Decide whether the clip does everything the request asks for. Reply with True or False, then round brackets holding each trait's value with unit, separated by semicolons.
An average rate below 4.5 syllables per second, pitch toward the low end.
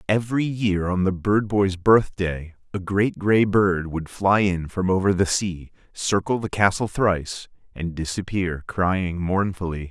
True (4.1 syllables/s; 95 Hz)